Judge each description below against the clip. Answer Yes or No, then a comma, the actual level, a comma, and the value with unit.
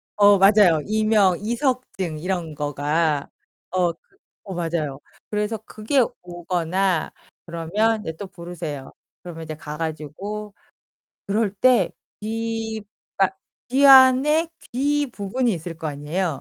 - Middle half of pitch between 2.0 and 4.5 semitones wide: No, average, 5.2 semitones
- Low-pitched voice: No, high, 190 Hz